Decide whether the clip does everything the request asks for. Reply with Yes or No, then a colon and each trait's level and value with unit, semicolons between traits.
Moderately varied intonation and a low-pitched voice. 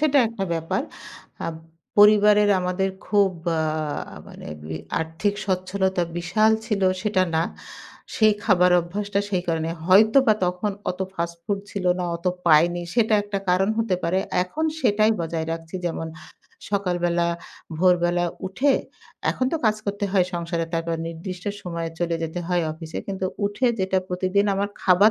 No: average, 3.3 semitones; medium, 185 Hz